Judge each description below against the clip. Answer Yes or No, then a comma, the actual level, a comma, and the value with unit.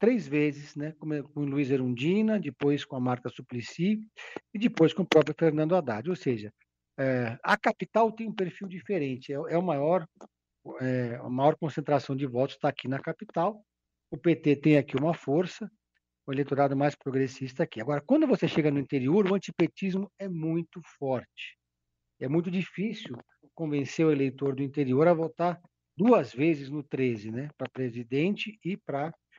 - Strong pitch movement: No, average, 4.8 semitones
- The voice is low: No, medium, 150 Hz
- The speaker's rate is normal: Yes, average, 170 wpm